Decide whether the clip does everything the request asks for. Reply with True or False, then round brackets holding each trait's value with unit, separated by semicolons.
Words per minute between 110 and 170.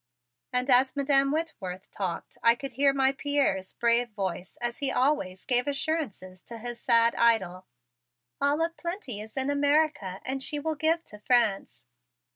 True (160 wpm)